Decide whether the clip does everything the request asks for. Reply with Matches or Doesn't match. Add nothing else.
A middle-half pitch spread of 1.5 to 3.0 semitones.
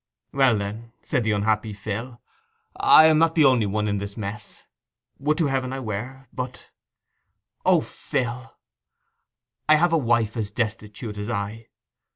Doesn't match